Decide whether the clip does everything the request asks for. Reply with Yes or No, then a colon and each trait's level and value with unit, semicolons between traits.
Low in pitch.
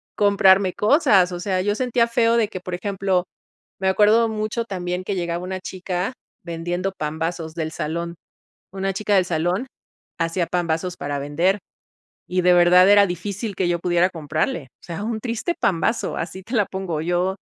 No: medium, 185 Hz